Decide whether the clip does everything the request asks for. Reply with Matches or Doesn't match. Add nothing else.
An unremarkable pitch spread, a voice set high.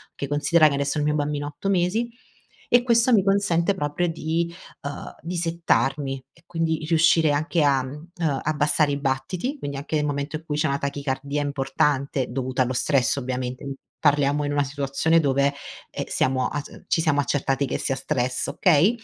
Doesn't match